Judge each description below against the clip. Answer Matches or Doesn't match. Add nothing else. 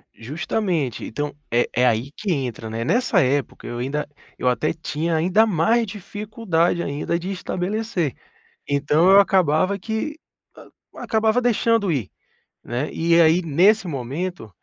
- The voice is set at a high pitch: Doesn't match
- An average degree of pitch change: Doesn't match